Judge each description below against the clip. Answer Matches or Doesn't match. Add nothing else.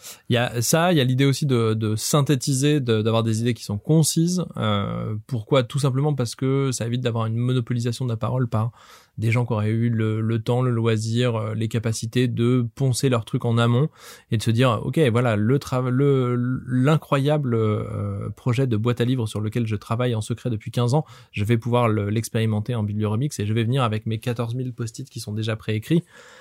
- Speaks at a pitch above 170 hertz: Doesn't match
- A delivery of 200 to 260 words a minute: Matches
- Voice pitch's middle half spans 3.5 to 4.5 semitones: Doesn't match